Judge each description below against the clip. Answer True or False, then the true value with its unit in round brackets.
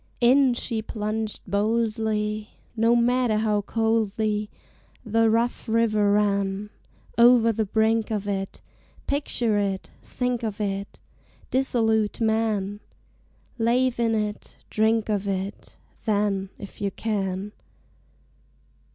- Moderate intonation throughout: False (1.8 semitones)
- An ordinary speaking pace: False (110 wpm)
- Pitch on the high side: True (220 Hz)